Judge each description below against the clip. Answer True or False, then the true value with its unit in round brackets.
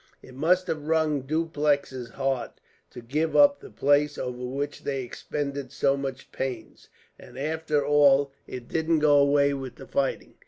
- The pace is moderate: True (160 wpm)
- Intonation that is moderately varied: False (2.2 semitones)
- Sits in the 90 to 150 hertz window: True (140 Hz)